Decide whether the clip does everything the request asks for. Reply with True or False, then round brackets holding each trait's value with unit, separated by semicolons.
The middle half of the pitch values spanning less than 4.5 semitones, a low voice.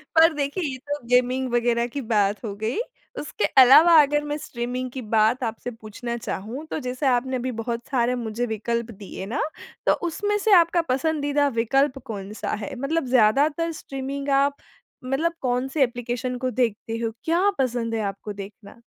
False (3.7 semitones; 250 Hz)